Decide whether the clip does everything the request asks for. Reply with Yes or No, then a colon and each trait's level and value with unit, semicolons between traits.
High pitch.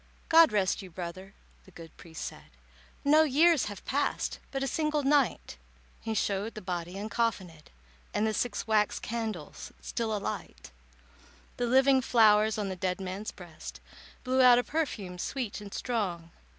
Yes: high, 215 Hz